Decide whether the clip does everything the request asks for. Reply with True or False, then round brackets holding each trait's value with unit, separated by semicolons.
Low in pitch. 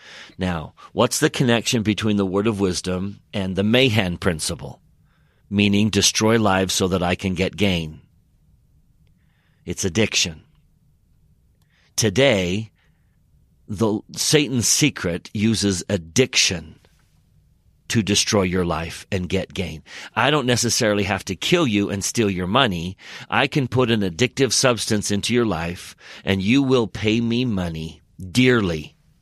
True (100 Hz)